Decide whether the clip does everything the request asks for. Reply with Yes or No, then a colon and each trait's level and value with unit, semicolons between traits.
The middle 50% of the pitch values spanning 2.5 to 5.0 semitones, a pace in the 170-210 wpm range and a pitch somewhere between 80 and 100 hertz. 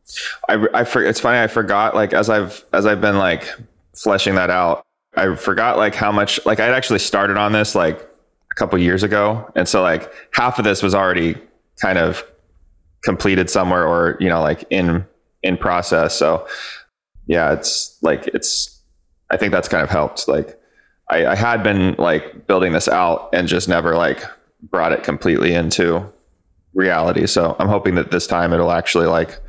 Yes: average, 3.2 semitones; average, 185 wpm; very low, 90 Hz